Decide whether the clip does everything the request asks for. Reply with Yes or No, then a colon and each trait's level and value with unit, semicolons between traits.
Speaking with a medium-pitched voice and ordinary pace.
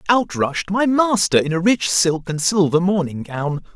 Yes: medium, 180 Hz; average, 190 wpm